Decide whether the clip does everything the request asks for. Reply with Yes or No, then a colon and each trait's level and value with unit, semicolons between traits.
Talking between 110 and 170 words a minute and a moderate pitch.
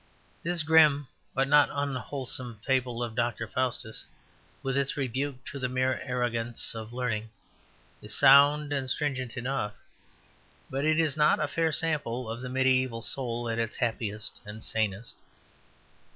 No: average, 145 wpm; low, 130 Hz